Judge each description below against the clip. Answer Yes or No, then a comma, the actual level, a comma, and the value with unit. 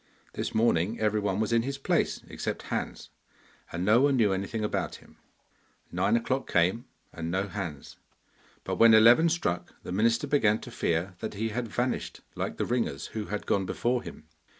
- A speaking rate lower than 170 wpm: No, average, 175 wpm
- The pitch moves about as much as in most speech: Yes, average, 3.6 semitones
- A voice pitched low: Yes, low, 110 Hz